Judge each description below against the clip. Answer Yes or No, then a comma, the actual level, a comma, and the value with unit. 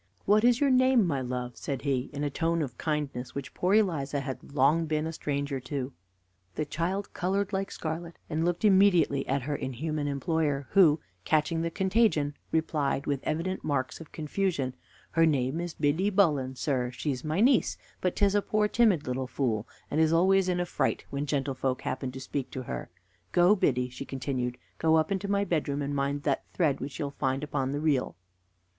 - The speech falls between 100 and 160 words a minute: No, average, 190 wpm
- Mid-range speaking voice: Yes, medium, 150 Hz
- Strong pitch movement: No, average, 4.5 semitones